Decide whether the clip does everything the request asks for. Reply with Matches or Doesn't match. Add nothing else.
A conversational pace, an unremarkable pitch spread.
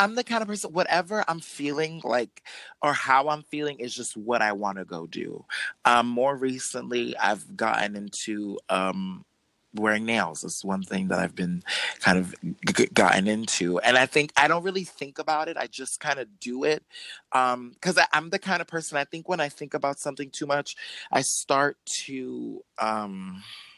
Doesn't match